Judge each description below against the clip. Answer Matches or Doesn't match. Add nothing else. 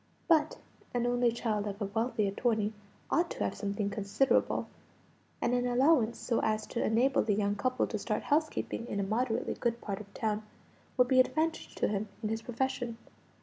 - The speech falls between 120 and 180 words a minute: Doesn't match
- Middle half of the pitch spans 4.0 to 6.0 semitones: Doesn't match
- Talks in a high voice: Matches